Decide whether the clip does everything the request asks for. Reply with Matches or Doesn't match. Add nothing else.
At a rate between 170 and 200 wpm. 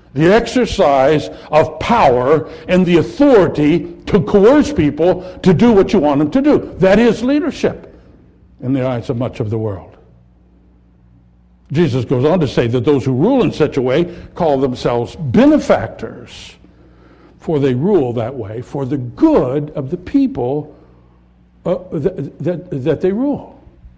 Doesn't match